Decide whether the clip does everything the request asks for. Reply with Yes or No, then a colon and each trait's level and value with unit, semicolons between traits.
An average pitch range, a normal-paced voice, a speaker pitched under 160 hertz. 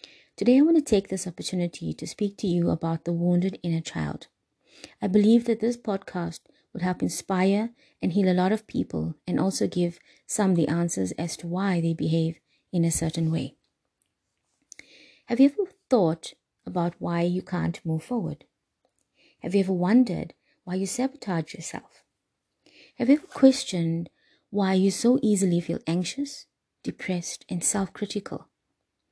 No: average, 4.0 semitones; average, 160 wpm; medium, 185 Hz